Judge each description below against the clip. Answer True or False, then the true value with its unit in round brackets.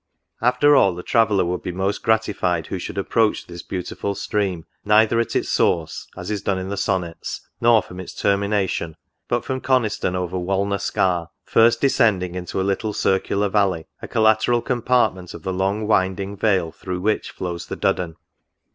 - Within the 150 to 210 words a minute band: True (175 wpm)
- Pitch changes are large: False (3.2 semitones)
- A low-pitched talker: True (100 Hz)